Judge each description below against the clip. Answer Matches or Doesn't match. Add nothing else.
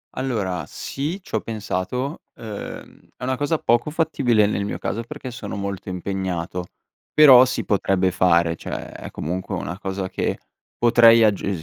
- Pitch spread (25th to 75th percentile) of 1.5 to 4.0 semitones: Doesn't match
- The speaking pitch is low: Matches